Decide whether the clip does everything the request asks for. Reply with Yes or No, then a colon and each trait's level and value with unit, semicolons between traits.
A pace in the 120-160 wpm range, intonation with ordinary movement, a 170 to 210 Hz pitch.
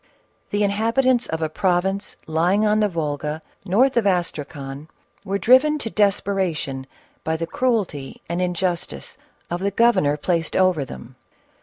Yes: average, 140 wpm; average, 4.9 semitones; medium, 185 Hz